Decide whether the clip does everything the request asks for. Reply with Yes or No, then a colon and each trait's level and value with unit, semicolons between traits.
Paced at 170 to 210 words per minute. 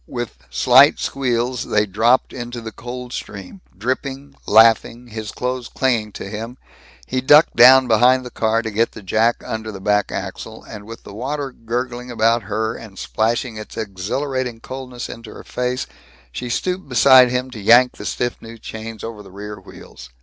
Yes: average, 175 wpm